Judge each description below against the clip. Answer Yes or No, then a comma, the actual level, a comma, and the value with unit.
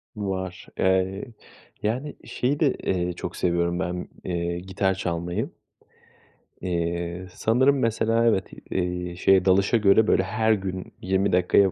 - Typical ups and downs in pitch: Yes, average, 3.3 semitones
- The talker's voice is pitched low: Yes, very low, 95 Hz